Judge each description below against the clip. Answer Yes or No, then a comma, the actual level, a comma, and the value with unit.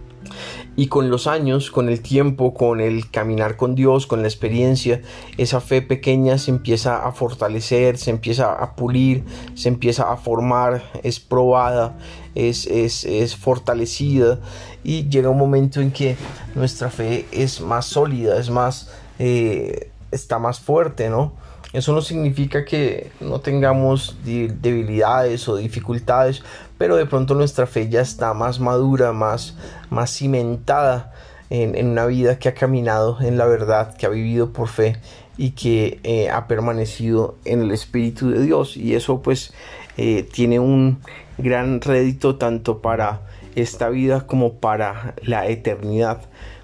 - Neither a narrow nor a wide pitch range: No, narrow, 2.2 semitones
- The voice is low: Yes, low, 120 Hz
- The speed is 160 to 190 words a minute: No, average, 150 wpm